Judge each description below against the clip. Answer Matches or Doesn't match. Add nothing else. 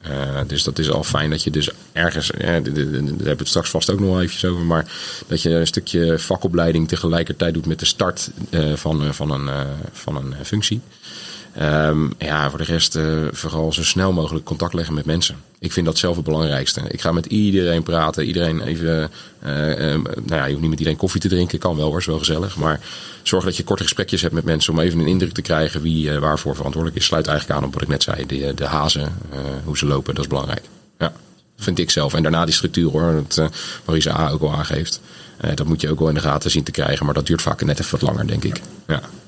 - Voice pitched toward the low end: Matches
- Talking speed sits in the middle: Doesn't match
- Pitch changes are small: Matches